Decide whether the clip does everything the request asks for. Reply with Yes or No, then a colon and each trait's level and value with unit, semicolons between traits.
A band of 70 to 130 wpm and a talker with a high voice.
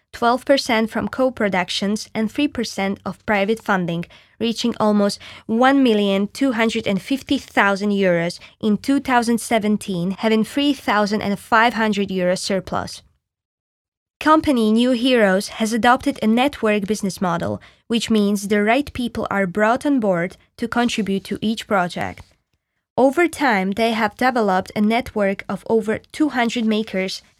Yes: slow, 110 wpm; high, 220 Hz